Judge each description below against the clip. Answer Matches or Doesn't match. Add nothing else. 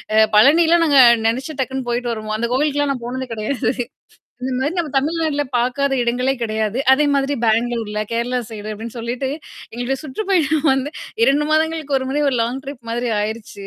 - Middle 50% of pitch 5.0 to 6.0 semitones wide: Doesn't match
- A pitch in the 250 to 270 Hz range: Matches